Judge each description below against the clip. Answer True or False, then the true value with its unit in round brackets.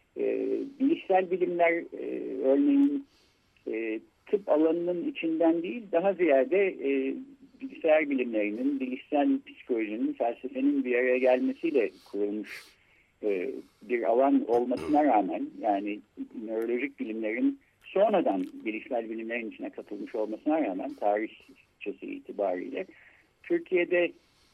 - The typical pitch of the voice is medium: True (175 Hz)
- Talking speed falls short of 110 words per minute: True (100 wpm)